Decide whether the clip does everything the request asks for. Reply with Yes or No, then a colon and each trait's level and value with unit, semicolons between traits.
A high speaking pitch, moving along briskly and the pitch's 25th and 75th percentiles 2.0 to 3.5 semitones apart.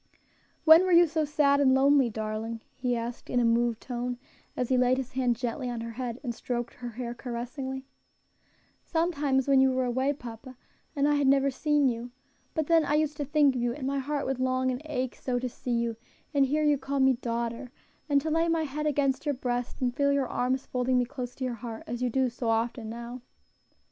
Yes: very high, 260 Hz; fast, 225 wpm; average, 2.7 semitones